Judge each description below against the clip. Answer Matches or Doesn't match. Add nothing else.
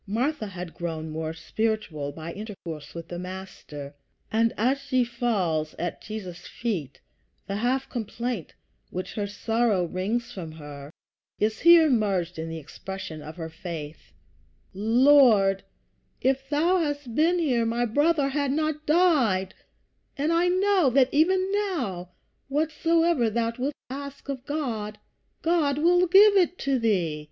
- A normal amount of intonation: Doesn't match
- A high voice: Matches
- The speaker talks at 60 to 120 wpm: Doesn't match